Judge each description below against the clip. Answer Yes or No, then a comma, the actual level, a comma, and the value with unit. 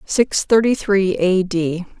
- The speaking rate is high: No, average, 150 wpm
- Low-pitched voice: No, high, 190 Hz